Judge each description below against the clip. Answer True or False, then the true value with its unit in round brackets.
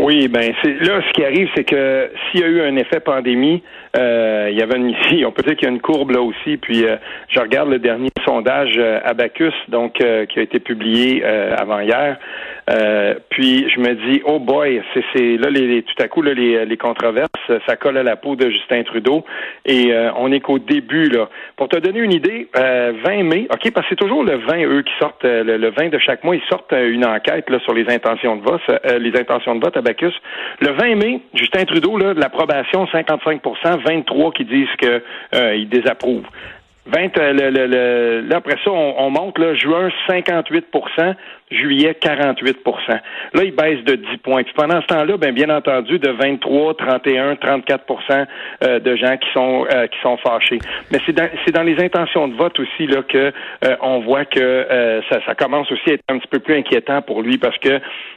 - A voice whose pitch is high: False (135 Hz)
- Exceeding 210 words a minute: True (220 wpm)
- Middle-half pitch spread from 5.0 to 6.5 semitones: False (4.5 semitones)